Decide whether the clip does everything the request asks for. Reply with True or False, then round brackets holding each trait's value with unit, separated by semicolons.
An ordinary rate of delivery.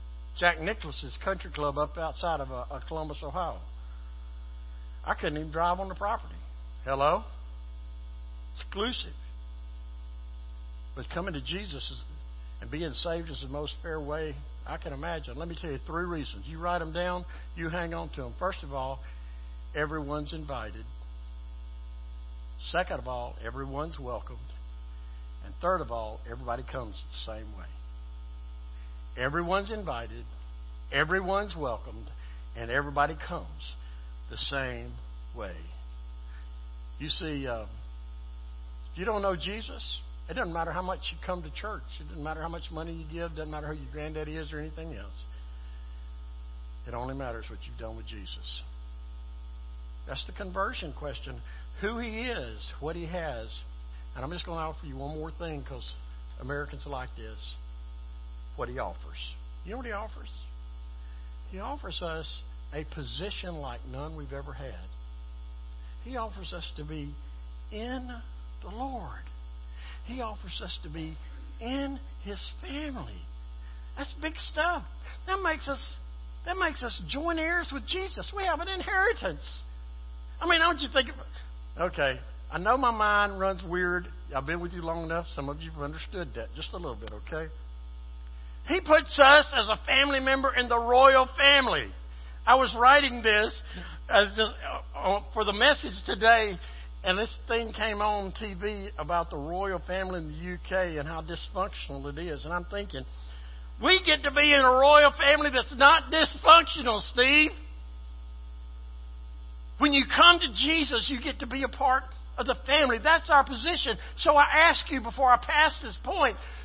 True (160 wpm)